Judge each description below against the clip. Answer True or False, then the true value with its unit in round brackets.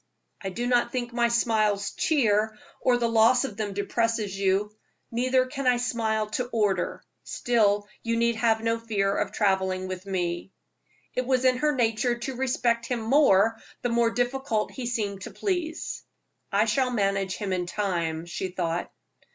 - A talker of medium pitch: False (225 Hz)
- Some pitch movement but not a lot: True (3.6 semitones)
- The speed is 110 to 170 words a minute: True (165 wpm)